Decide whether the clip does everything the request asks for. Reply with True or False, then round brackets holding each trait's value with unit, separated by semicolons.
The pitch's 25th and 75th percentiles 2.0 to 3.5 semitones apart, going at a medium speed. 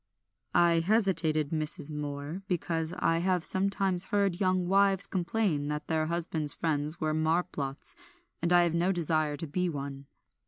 True (3.0 semitones; 150 wpm)